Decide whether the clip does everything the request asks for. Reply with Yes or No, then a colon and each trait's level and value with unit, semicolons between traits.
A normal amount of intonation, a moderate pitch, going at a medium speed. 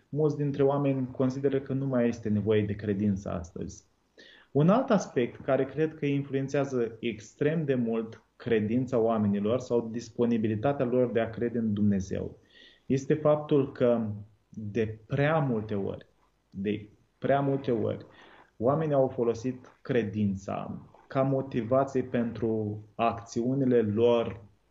No: average, 3.8 semitones; low, 120 Hz; average, 125 wpm